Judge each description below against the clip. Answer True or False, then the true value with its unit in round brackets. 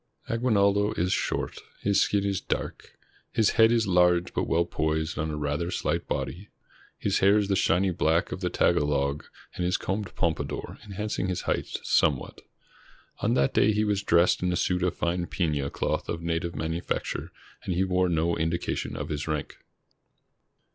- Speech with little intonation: False (3.3 semitones)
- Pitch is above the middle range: False (90 Hz)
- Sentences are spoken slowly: False (180 wpm)